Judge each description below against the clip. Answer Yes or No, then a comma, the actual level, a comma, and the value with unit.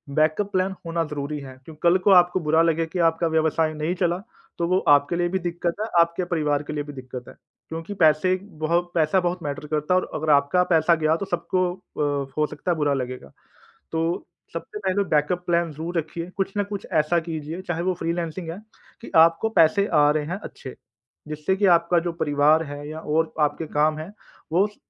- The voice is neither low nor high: Yes, medium, 165 Hz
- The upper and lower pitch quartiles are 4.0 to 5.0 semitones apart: No, narrow, 2.6 semitones